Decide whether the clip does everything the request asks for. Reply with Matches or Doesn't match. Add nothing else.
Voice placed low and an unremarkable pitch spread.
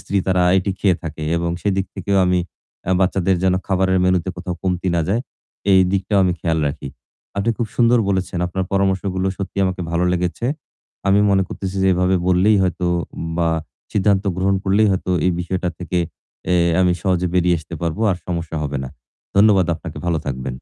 Doesn't match